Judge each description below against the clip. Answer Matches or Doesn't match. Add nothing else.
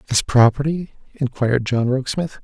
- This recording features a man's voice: Matches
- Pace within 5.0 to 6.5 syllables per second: Matches